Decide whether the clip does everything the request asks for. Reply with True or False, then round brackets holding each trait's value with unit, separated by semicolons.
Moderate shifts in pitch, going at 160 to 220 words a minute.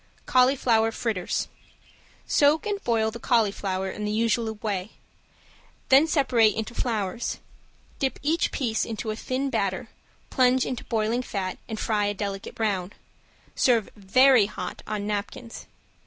False (3.4 semitones; 135 wpm)